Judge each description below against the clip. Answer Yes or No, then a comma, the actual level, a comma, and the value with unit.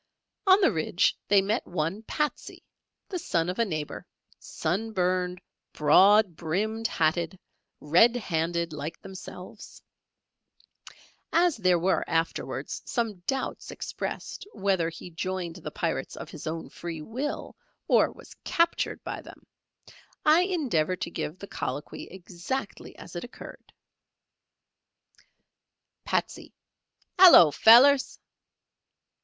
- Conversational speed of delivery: No, slow, 115 wpm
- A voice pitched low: No, medium, 185 Hz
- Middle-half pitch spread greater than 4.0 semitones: Yes, wide, 5.5 semitones